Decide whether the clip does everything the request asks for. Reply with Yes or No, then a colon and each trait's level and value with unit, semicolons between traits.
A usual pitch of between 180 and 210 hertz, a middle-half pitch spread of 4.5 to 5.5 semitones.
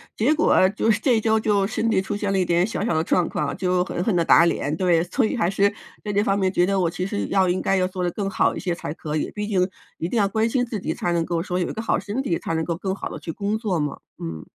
No: high, 190 Hz; average, 3.2 semitones